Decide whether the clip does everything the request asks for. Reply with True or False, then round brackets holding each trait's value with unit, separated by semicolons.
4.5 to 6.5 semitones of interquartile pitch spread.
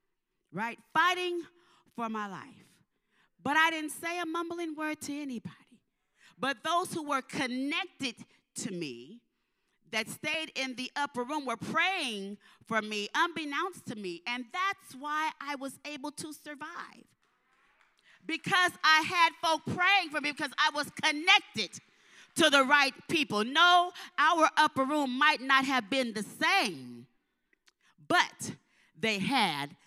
True (5.0 semitones)